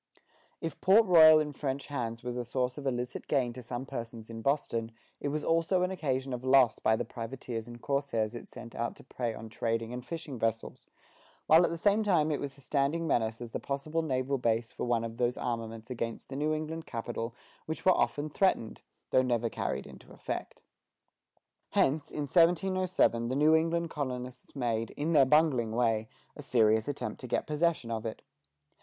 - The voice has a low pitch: Yes, low, 130 Hz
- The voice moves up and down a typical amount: Yes, average, 4.8 semitones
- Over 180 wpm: Yes, average, 195 wpm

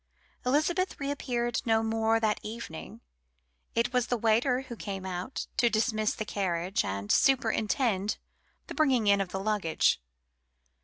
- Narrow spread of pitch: No, average, 3.9 semitones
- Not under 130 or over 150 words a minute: Yes, average, 140 wpm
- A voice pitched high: Yes, high, 220 Hz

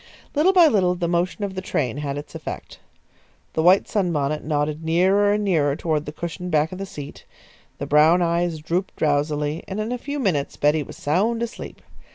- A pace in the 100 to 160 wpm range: No, average, 195 wpm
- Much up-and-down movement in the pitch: No, average, 4.6 semitones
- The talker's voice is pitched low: No, medium, 170 Hz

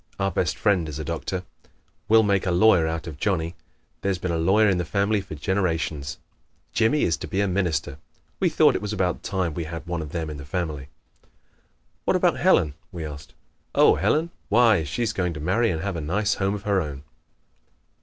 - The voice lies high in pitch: No, very low, 90 Hz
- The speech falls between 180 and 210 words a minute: Yes, fast, 205 wpm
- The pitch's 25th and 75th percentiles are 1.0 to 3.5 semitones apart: No, average, 4.0 semitones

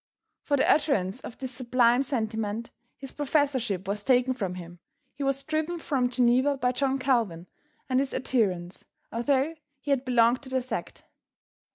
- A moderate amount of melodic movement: Yes, average, 3.2 semitones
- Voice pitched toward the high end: Yes, very high, 255 Hz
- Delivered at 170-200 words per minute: No, average, 160 wpm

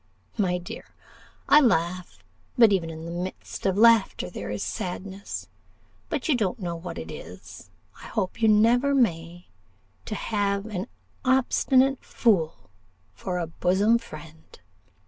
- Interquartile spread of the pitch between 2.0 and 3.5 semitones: No, average, 4.7 semitones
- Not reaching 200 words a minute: Yes, average, 140 wpm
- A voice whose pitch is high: Yes, high, 195 Hz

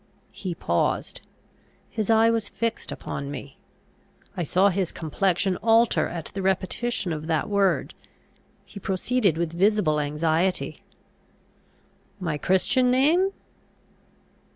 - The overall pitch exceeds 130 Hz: Yes, high, 190 Hz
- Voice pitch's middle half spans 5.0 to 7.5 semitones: Yes, average, 5.3 semitones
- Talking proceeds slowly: Yes, slow, 110 wpm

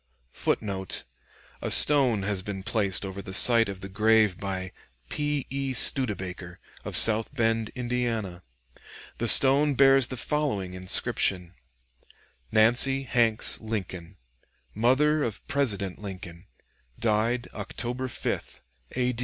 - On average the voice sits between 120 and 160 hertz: No, low, 110 Hz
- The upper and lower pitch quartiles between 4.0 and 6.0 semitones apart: Yes, average, 4.7 semitones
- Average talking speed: No, slow, 115 wpm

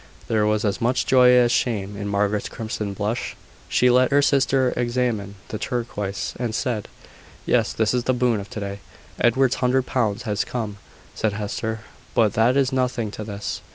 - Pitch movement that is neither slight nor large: Yes, average, 3.2 semitones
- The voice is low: Yes, low, 115 Hz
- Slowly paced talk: No, average, 180 wpm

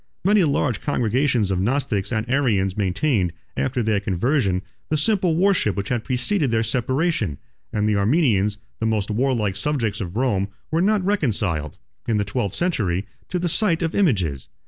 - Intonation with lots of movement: Yes, wide, 6.9 semitones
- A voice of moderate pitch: No, low, 115 Hz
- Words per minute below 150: No, average, 165 wpm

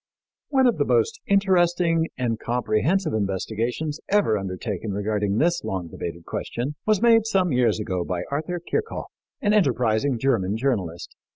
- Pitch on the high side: No, low, 125 Hz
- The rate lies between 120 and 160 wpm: Yes, average, 145 wpm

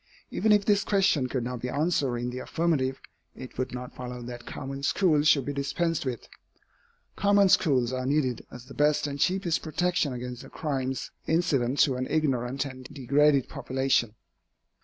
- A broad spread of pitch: No, average, 3.8 semitones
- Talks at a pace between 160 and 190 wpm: Yes, average, 170 wpm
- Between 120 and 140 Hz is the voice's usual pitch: Yes, low, 135 Hz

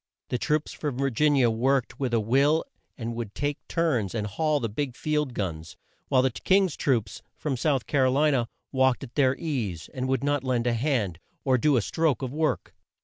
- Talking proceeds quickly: Yes, fast, 215 wpm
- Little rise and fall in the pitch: No, average, 3.8 semitones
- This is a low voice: Yes, low, 130 Hz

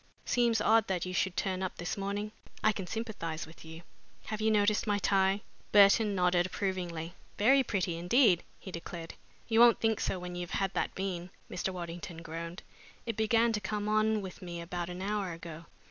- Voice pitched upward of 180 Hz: Yes, high, 190 Hz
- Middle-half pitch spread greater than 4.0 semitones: No, average, 3.4 semitones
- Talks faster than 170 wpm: Yes, average, 190 wpm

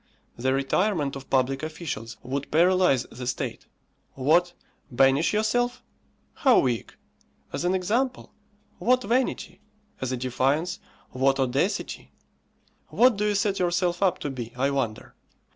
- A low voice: No, medium, 155 Hz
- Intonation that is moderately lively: No, wide, 6.8 semitones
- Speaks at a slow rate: Yes, slow, 130 wpm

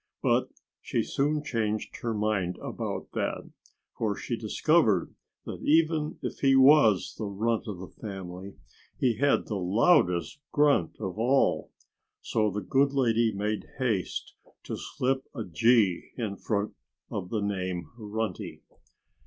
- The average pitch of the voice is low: Yes, low, 110 Hz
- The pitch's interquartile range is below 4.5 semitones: No, average, 5.0 semitones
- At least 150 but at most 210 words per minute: No, slow, 135 wpm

